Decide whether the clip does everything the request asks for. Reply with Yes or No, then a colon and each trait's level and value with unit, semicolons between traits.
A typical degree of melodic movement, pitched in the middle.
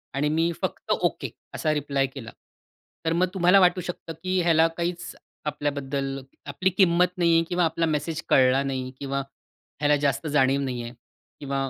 Yes: average, 3.8 semitones; medium, 150 Hz